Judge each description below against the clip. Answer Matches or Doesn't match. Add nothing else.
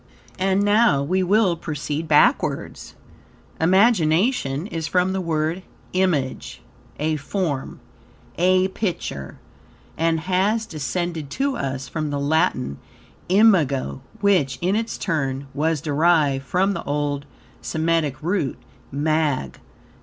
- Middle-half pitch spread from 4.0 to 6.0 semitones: Matches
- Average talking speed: Doesn't match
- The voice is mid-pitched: Matches